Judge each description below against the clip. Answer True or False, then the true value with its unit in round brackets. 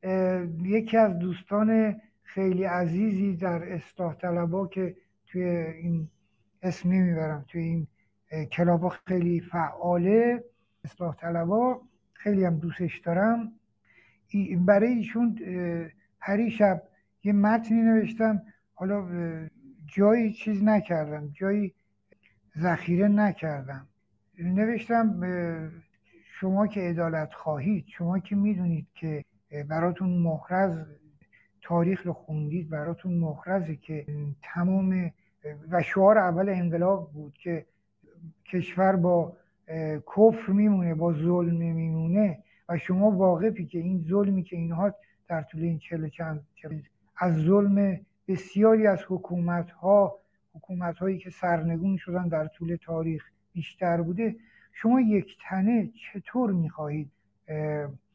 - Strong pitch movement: False (3.4 semitones)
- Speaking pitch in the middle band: True (175 Hz)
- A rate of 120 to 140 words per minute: False (105 wpm)